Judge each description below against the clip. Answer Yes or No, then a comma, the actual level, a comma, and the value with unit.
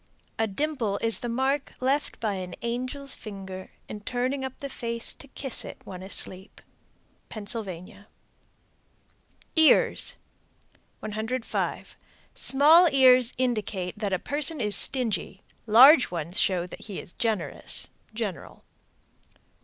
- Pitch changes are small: No, average, 4.9 semitones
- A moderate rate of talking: No, slow, 120 wpm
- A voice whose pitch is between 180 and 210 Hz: No, high, 230 Hz